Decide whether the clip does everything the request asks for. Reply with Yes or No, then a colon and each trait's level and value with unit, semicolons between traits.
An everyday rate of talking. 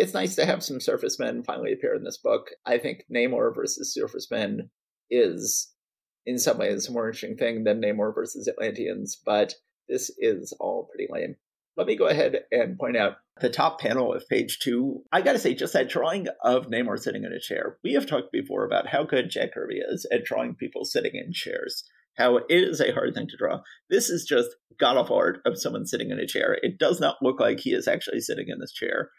No: fast, 225 wpm